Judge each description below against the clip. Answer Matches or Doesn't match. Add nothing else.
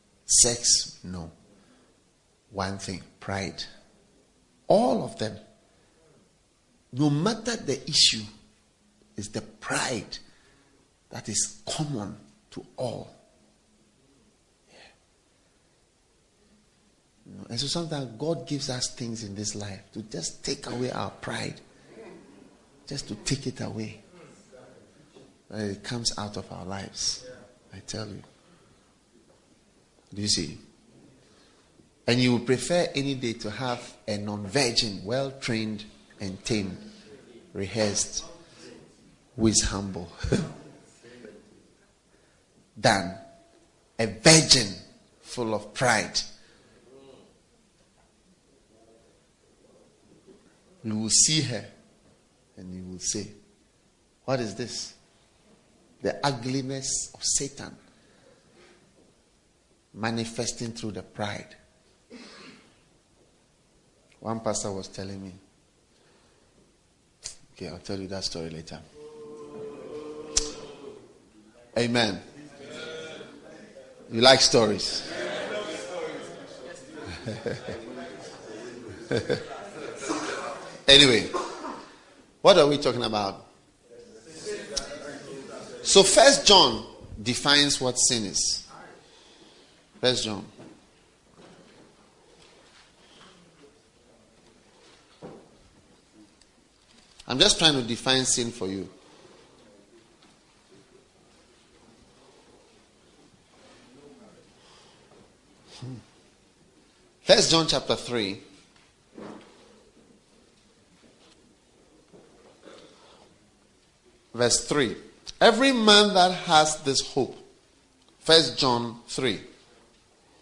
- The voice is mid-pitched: Doesn't match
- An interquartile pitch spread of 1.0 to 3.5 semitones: Doesn't match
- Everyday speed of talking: Doesn't match